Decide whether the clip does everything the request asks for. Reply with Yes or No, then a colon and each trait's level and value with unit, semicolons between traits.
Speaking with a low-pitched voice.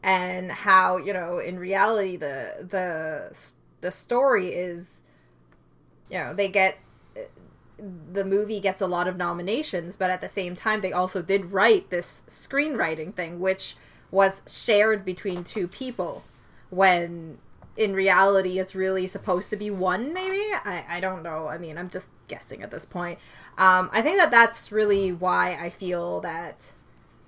No: medium, 185 Hz